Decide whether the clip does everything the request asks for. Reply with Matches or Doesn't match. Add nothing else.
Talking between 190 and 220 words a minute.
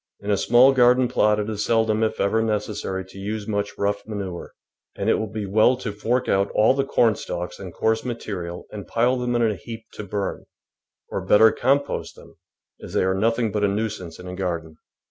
Matches